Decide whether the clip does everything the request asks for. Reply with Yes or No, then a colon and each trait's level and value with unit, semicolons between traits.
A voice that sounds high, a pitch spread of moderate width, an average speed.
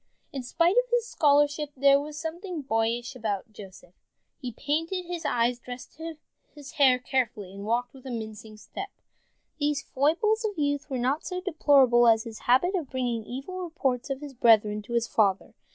Yes: very high, 265 Hz; average, 4.9 semitones; average, 175 wpm